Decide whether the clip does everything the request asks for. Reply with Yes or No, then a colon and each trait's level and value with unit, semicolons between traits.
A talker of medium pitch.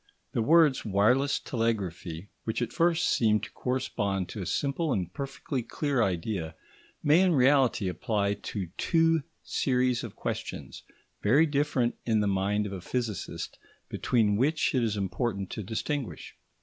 No: low, 115 Hz